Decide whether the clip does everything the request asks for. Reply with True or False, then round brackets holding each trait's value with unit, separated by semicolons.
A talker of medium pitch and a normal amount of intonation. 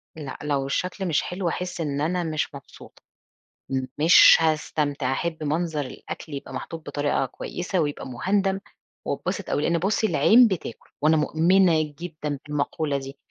True (155 Hz; 3.5 semitones)